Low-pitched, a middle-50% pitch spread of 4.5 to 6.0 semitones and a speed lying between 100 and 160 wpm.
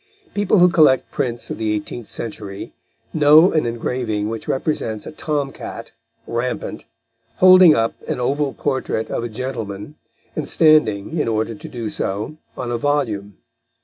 Yes: low, 125 Hz; wide, 5.4 semitones; average, 150 wpm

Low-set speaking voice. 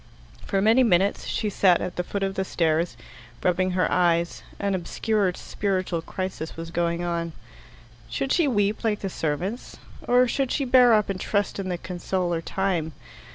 No: medium, 185 Hz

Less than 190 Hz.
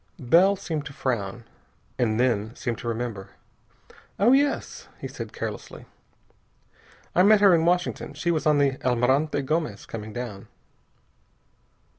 Yes: low, 135 Hz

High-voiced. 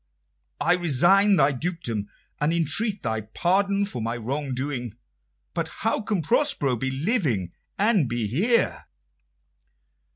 No: medium, 155 Hz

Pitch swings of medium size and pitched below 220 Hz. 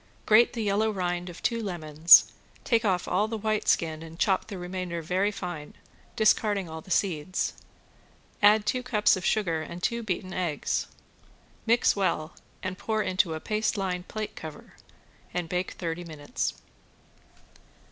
Yes: average, 3.9 semitones; medium, 185 Hz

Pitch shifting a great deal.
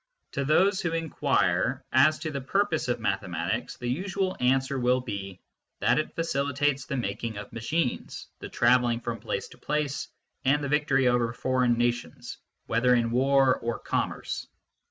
No: average, 3.7 semitones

